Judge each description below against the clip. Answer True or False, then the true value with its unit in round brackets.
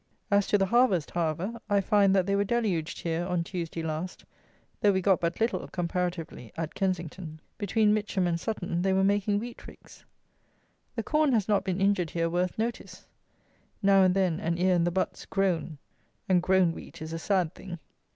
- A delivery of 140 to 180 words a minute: False (190 wpm)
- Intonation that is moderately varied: True (3.0 semitones)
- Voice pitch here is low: False (185 Hz)